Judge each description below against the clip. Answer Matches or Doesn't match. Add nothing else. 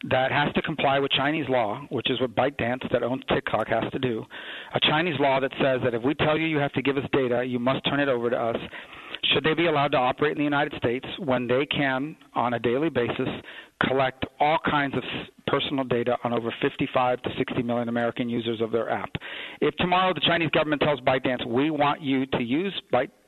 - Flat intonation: Doesn't match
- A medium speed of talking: Doesn't match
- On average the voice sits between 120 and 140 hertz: Matches